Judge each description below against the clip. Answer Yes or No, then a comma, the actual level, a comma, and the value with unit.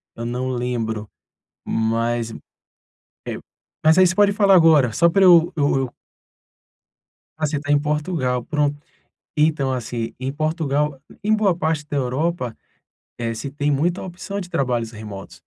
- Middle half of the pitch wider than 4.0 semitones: Yes, average, 5.1 semitones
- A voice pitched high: No, medium, 145 Hz